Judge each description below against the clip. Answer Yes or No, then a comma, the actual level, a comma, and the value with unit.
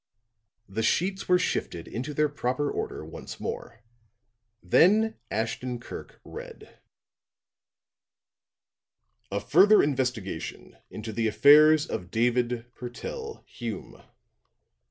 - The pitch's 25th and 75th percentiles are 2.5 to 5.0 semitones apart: No, wide, 5.6 semitones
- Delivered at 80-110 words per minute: Yes, slow, 95 wpm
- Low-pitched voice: Yes, low, 125 Hz